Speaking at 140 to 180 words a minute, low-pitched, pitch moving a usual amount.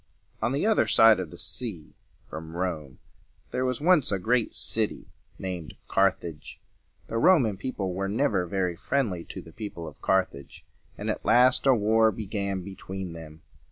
Yes: average, 170 wpm; low, 100 Hz; average, 4.6 semitones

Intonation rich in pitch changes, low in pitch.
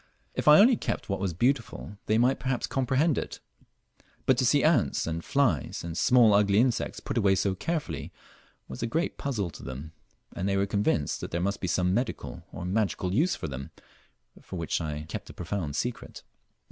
Yes: wide, 6.7 semitones; low, 100 Hz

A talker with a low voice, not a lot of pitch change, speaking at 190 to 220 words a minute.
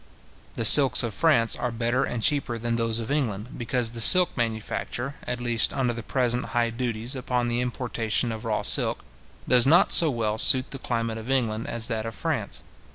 Yes: low, 120 Hz; narrow, 1.9 semitones; average, 195 wpm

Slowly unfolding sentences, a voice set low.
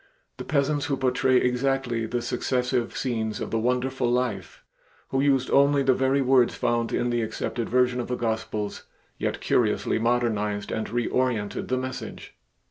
No: average, 155 wpm; low, 125 Hz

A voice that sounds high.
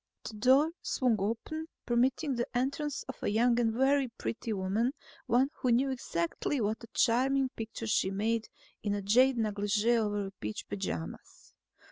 Yes: high, 230 Hz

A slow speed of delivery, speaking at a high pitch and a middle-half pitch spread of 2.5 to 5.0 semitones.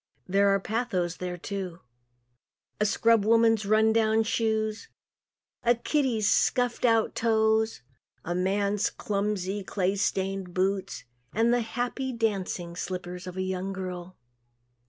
Yes: slow, 125 wpm; high, 205 Hz; average, 3.1 semitones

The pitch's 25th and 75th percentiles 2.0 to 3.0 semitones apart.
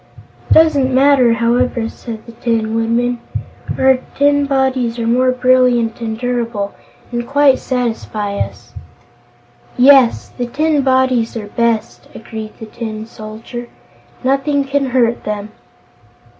Yes: narrow, 2.6 semitones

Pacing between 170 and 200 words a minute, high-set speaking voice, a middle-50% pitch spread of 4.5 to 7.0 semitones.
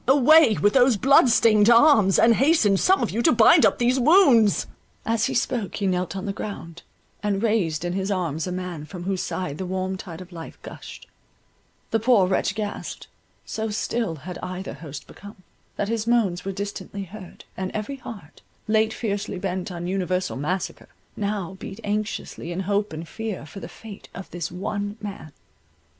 No: average, 180 wpm; high, 200 Hz; average, 3.5 semitones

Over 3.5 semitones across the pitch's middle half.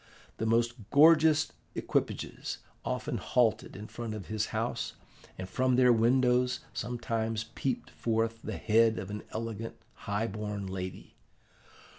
No: narrow, 2.4 semitones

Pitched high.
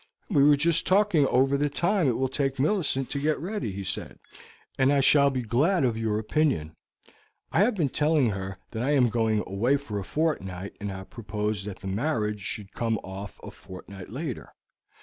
No: low, 130 Hz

